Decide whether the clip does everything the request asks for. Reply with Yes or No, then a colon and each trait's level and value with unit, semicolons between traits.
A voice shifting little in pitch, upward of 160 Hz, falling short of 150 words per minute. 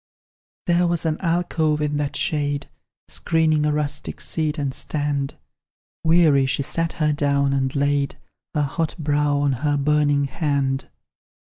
No: narrow, 1.7 semitones; medium, 145 Hz; average, 140 wpm